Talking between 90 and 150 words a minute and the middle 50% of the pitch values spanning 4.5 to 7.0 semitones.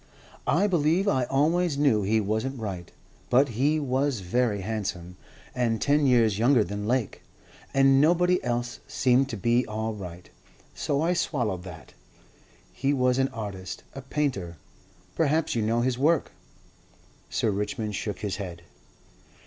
Yes: average, 145 wpm; average, 5.2 semitones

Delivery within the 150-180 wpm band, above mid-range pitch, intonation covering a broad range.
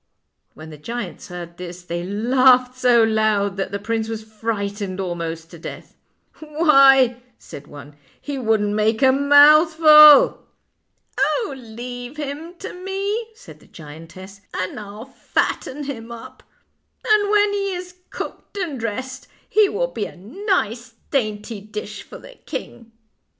Yes: average, 155 wpm; high, 235 Hz; wide, 6.6 semitones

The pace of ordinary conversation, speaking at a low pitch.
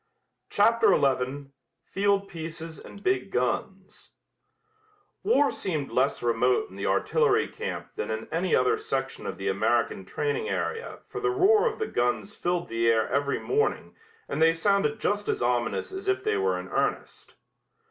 No: average, 160 wpm; high, 205 Hz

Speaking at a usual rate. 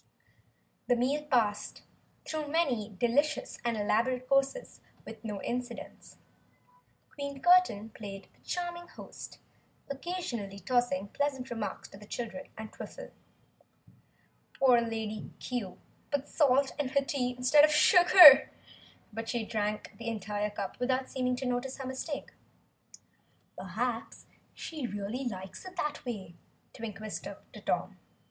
No: slow, 130 wpm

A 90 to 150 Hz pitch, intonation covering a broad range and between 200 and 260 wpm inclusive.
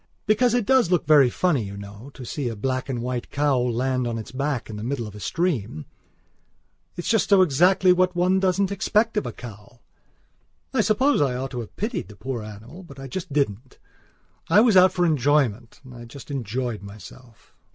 Yes: low, 135 Hz; wide, 7.5 semitones; fast, 205 wpm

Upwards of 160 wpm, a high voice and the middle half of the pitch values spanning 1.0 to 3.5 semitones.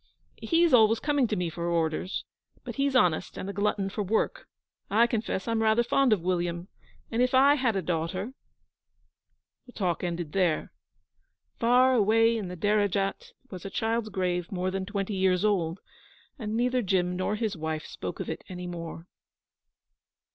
No: average, 170 wpm; high, 200 Hz; average, 4.4 semitones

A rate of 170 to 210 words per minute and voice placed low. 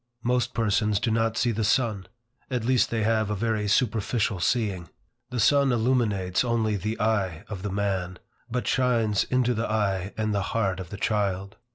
Yes: average, 180 wpm; low, 110 Hz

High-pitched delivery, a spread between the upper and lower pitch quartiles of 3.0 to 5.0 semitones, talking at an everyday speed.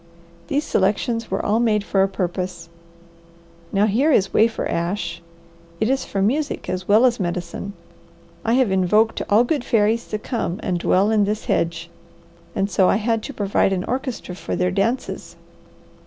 Yes: high, 205 Hz; average, 3.7 semitones; average, 170 wpm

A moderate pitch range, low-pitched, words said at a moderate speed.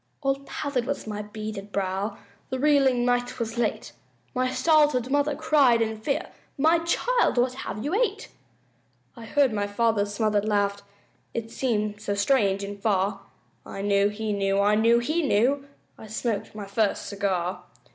No: average, 4.9 semitones; high, 225 Hz; average, 160 wpm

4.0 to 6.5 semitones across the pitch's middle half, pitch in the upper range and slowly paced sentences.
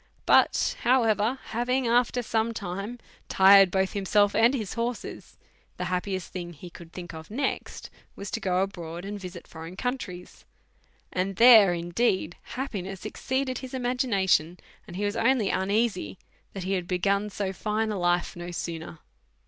No: average, 4.4 semitones; high, 195 Hz; average, 155 wpm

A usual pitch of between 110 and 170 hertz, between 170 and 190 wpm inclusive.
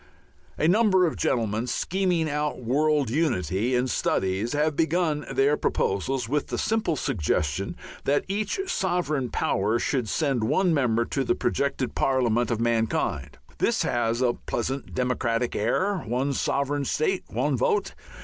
No: low, 135 Hz; average, 140 wpm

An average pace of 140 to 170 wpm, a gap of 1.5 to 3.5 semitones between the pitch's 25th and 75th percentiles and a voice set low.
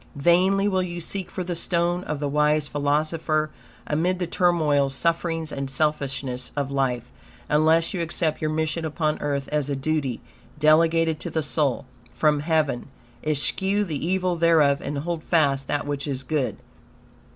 No: average, 160 wpm; average, 2.8 semitones; medium, 155 Hz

